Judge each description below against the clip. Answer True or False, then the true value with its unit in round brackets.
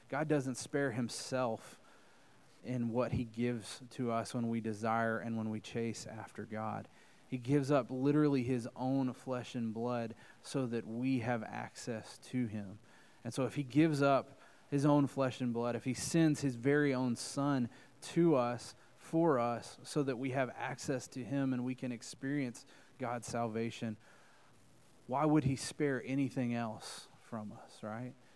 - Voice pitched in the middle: False (125 Hz)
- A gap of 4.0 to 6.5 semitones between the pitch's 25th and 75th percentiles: False (2.9 semitones)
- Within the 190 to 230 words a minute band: False (165 wpm)